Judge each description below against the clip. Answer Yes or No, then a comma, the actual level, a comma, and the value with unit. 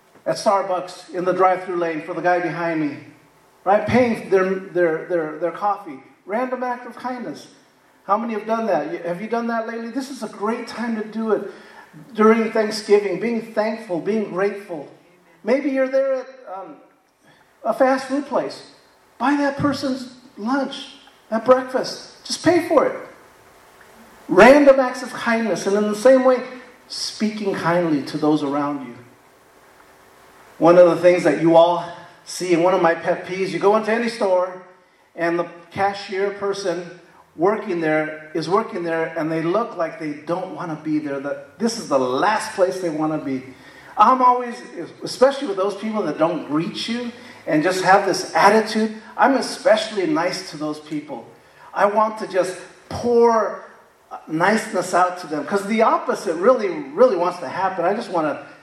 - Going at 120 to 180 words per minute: Yes, average, 175 wpm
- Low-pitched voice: No, high, 200 Hz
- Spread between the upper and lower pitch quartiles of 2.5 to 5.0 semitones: No, wide, 5.4 semitones